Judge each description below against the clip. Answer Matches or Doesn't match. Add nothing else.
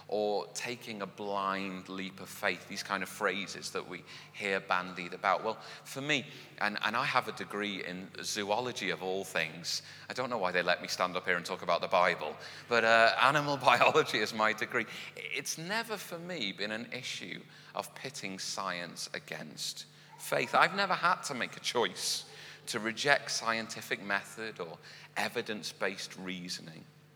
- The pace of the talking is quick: Doesn't match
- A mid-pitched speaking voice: Doesn't match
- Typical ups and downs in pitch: Matches